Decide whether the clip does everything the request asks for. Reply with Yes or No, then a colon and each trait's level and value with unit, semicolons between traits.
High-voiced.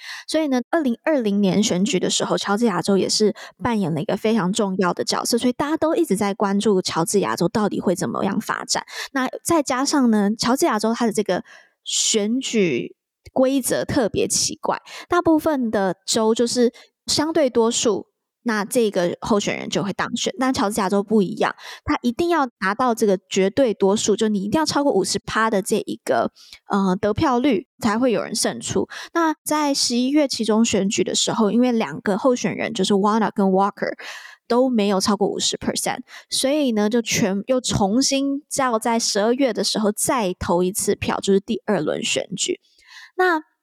Yes: high, 220 Hz